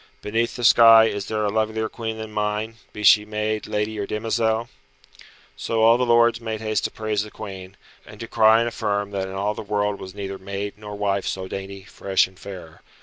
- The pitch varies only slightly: Yes, narrow, 1.8 semitones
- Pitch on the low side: Yes, low, 105 Hz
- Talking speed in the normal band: No, fast, 210 wpm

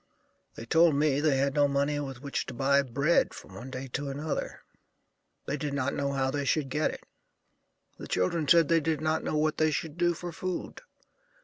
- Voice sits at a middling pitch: Yes, medium, 145 Hz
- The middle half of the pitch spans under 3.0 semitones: Yes, narrow, 2.4 semitones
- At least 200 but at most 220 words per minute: Yes, fast, 205 wpm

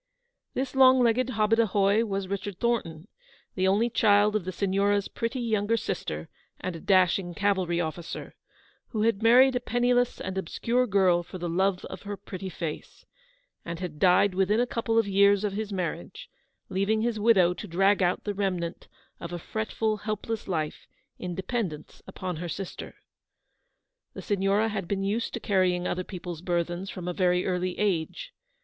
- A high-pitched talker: Yes, high, 195 Hz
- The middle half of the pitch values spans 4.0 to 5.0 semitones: No, average, 3.4 semitones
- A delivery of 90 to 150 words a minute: No, average, 170 wpm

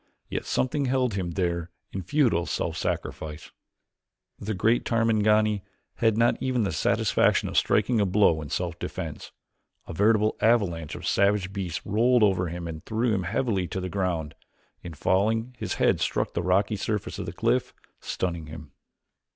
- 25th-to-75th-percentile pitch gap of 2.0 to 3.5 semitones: No, average, 4.5 semitones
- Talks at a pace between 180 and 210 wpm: No, average, 165 wpm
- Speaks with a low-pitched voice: Yes, low, 100 Hz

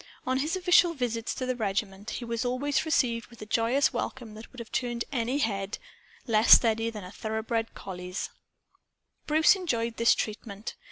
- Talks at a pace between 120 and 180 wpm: Yes, average, 170 wpm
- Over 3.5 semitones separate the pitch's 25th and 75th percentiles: No, average, 2.9 semitones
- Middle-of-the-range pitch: No, high, 230 Hz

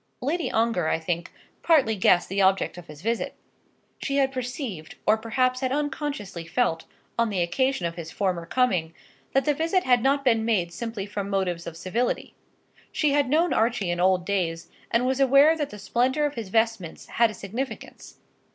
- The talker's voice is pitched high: Yes, high, 225 Hz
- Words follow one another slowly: No, average, 185 wpm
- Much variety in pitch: Yes, wide, 6.4 semitones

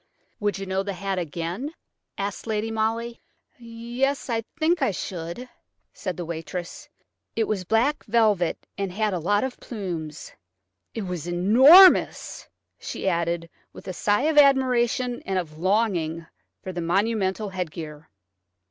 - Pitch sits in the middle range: No, high, 200 Hz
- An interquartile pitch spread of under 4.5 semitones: No, average, 5.0 semitones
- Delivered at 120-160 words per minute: Yes, average, 140 wpm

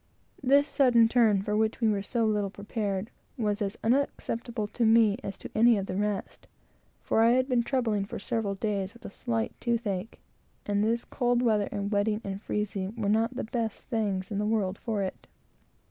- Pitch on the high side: Yes, high, 215 Hz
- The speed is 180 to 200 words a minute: Yes, average, 195 wpm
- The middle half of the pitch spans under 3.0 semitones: Yes, narrow, 2.5 semitones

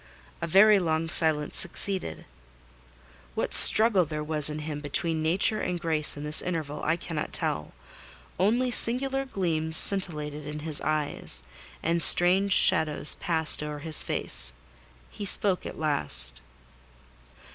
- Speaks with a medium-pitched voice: Yes, medium, 160 Hz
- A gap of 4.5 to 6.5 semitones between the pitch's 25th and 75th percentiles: No, average, 3.7 semitones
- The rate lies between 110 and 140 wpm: Yes, slow, 135 wpm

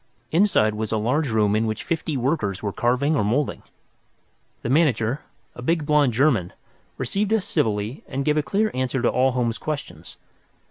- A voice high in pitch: No, low, 130 Hz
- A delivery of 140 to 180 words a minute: Yes, average, 175 wpm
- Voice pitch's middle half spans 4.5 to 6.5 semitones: Yes, wide, 5.4 semitones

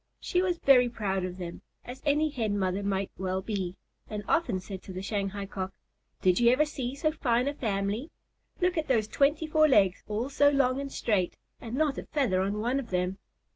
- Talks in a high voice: Yes, high, 225 Hz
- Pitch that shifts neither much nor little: No, wide, 6.4 semitones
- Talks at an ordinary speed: No, fast, 210 wpm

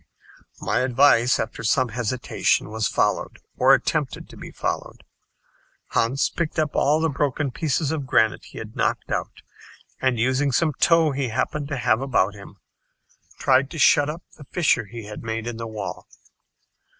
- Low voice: Yes, low, 130 Hz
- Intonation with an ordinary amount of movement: Yes, average, 4.2 semitones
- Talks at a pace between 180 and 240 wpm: No, average, 165 wpm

